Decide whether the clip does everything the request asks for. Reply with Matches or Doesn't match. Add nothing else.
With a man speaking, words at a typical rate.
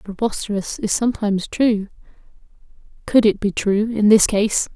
Doesn't match